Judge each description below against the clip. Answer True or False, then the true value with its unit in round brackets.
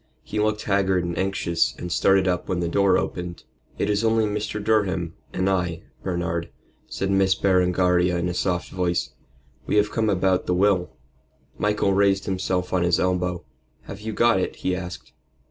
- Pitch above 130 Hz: False (95 Hz)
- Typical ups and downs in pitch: False (2.1 semitones)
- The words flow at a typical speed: True (175 wpm)